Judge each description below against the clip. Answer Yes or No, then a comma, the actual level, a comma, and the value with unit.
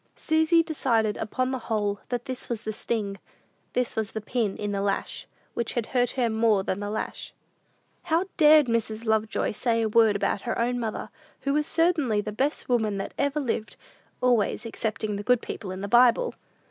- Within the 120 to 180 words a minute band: No, average, 190 wpm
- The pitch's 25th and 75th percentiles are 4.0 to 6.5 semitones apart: No, average, 3.2 semitones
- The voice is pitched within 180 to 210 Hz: No, high, 230 Hz